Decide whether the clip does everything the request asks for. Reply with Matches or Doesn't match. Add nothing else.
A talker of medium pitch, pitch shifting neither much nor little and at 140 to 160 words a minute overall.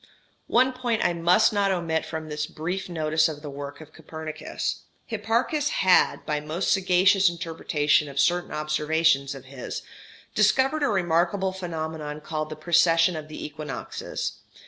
Matches